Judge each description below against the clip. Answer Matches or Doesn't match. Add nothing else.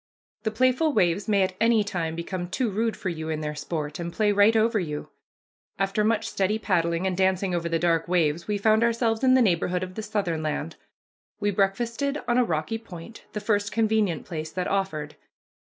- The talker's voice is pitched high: Matches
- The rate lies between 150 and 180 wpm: Doesn't match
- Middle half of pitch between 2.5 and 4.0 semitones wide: Doesn't match